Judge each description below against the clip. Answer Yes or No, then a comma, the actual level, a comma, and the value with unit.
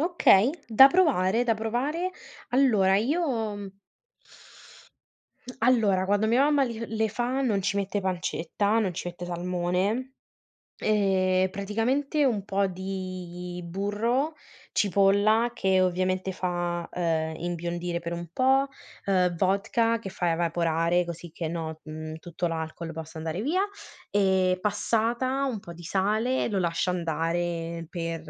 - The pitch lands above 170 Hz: Yes, high, 190 Hz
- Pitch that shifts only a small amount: No, average, 4.5 semitones